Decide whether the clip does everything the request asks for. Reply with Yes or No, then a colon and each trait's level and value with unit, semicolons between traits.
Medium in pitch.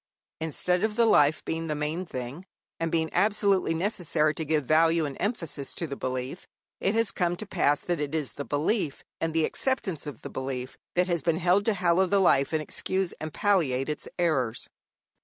Yes: medium, 165 Hz